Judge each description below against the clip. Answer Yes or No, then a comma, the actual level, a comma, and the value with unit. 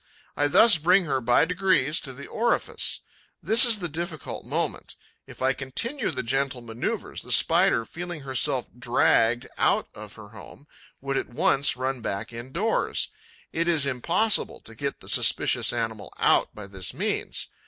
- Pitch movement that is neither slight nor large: No, wide, 6.2 semitones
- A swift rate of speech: No, average, 160 wpm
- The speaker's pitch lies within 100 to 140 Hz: Yes, low, 135 Hz